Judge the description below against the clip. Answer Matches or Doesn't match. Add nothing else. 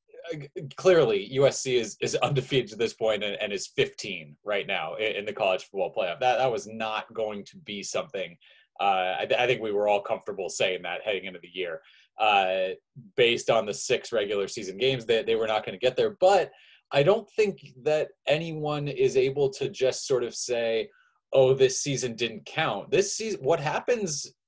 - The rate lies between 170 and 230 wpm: Matches